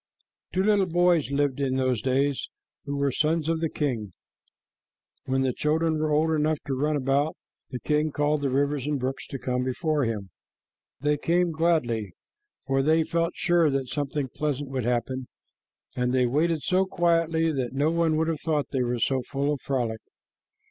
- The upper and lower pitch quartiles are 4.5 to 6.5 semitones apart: No, average, 3.5 semitones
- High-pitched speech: No, medium, 145 Hz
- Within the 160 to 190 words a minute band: Yes, average, 180 wpm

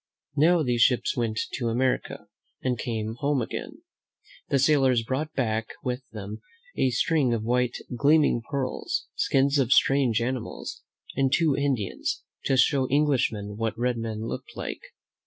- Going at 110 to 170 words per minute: Yes, average, 150 wpm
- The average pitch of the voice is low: Yes, low, 125 Hz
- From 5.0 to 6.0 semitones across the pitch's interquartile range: No, average, 3.4 semitones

